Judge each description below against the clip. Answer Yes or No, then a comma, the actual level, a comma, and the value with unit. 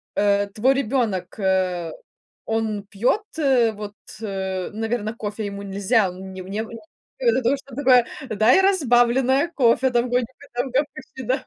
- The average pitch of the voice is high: Yes, high, 225 Hz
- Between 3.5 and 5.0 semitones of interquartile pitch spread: Yes, average, 4.4 semitones